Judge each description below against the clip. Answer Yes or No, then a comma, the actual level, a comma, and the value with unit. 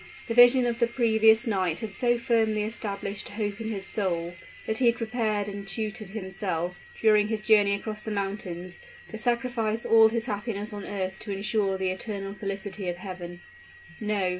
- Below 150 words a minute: No, average, 175 wpm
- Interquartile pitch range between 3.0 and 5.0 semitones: No, narrow, 2.4 semitones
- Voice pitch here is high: Yes, high, 210 Hz